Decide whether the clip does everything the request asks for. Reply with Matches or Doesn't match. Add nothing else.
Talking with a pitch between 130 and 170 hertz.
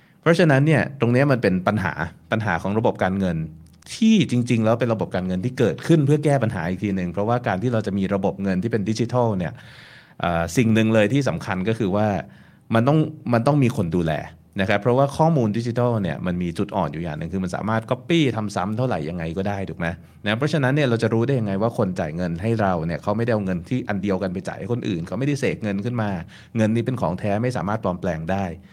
Doesn't match